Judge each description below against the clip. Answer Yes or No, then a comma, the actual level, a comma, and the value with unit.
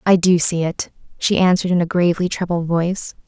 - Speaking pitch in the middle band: Yes, medium, 175 Hz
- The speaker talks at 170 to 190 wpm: No, average, 200 wpm